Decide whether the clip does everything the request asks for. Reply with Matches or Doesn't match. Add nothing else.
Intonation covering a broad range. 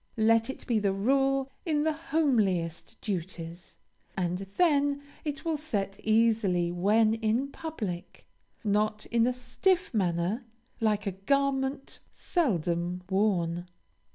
Matches